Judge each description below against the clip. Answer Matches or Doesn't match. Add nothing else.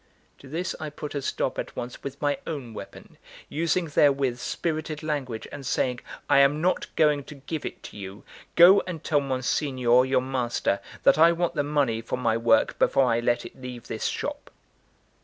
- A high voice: Doesn't match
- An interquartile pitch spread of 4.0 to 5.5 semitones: Doesn't match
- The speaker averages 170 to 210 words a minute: Matches